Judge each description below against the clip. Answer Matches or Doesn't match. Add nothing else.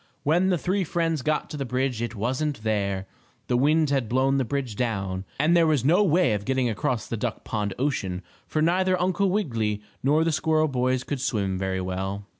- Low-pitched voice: Matches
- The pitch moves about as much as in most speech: Doesn't match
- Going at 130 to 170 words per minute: Doesn't match